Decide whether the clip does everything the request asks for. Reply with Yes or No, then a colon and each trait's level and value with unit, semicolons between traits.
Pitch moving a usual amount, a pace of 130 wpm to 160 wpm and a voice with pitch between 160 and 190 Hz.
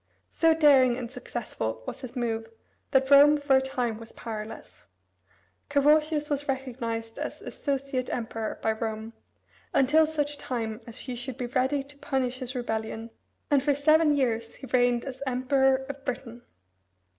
No: average, 3.3 semitones; average, 155 wpm; very high, 255 Hz